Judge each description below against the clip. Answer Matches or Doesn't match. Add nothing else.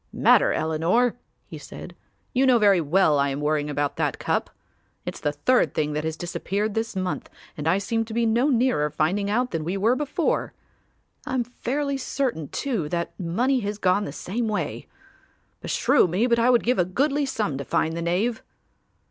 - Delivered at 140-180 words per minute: Doesn't match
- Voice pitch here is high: Matches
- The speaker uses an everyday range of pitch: Doesn't match